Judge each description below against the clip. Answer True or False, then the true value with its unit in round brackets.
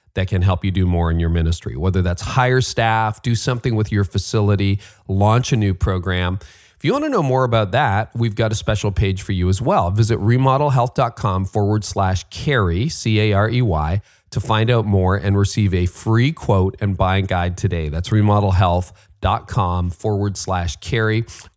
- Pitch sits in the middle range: False (100 Hz)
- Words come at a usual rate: True (175 wpm)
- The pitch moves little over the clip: False (3.3 semitones)